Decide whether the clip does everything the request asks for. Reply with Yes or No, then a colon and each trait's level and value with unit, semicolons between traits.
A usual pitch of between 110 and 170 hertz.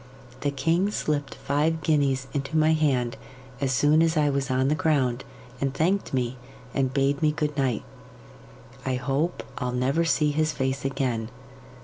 Yes: medium, 140 Hz